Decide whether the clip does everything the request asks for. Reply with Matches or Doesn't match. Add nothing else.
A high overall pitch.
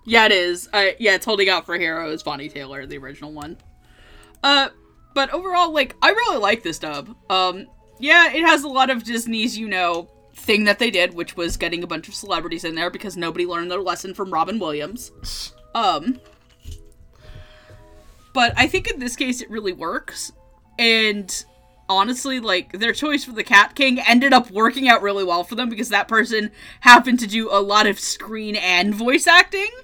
Matches